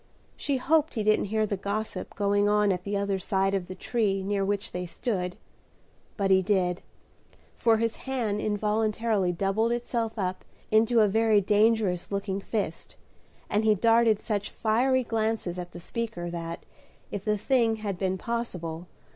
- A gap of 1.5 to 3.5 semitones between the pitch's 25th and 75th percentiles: Yes, average, 2.7 semitones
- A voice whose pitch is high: Yes, high, 210 Hz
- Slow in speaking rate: No, average, 165 wpm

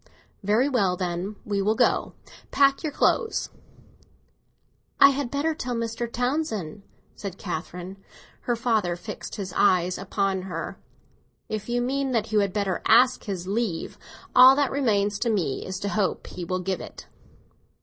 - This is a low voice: No, high, 210 Hz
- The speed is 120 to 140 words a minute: No, average, 160 wpm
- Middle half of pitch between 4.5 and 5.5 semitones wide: Yes, average, 4.8 semitones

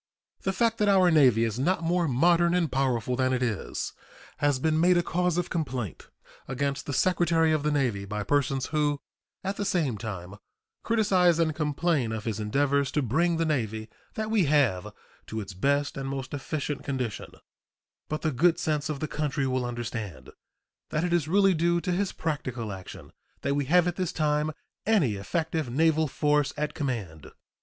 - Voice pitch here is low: No, medium, 145 Hz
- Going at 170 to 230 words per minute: Yes, average, 180 wpm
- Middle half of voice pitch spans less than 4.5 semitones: No, average, 5.1 semitones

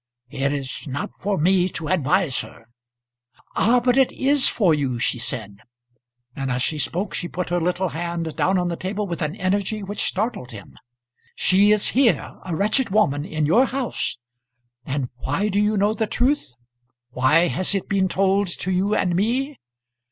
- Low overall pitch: No, medium, 185 Hz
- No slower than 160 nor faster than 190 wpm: Yes, average, 180 wpm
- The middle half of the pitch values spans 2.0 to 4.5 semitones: No, wide, 5.5 semitones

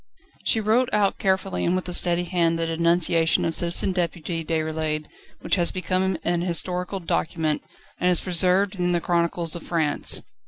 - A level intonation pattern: Yes, narrow, 1.8 semitones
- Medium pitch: Yes, medium, 175 Hz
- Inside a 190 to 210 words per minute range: No, average, 165 wpm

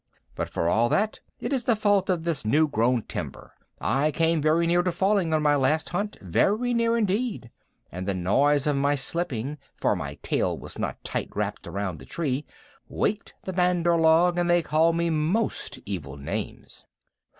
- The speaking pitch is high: No, medium, 160 Hz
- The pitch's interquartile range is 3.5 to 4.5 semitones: No, average, 5.0 semitones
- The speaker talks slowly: No, average, 185 wpm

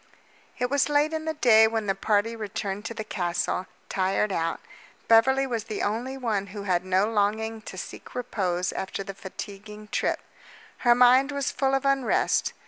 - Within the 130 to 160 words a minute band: No, average, 175 wpm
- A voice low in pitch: No, high, 220 Hz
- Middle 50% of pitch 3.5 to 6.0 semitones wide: Yes, average, 4.3 semitones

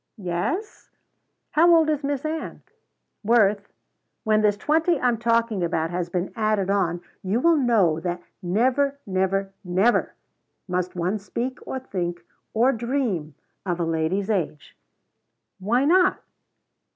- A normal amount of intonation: No, wide, 6.3 semitones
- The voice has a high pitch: Yes, high, 210 Hz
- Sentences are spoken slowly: Yes, slow, 130 wpm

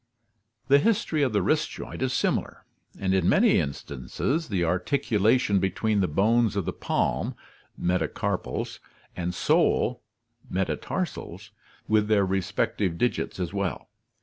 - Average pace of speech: No, slow, 125 wpm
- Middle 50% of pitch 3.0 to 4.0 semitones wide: No, average, 4.6 semitones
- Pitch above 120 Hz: No, low, 100 Hz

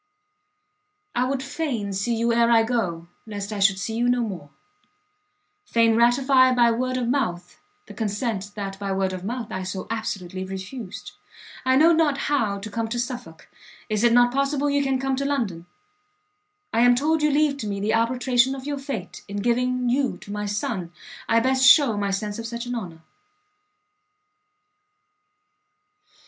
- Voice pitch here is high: Yes, high, 235 Hz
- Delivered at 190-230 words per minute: No, average, 175 wpm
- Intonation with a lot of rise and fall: No, average, 4.3 semitones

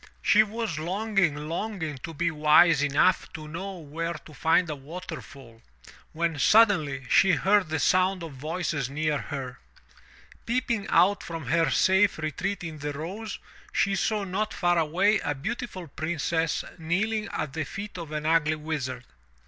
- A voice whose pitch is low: No, medium, 165 Hz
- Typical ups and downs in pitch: Yes, average, 4.3 semitones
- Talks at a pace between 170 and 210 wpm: No, average, 155 wpm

